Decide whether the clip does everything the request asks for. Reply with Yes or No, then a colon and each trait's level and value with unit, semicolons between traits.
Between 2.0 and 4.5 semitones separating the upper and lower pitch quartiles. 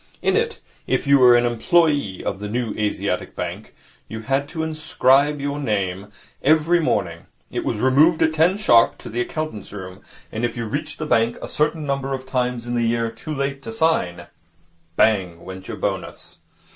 No: average, 5.3 semitones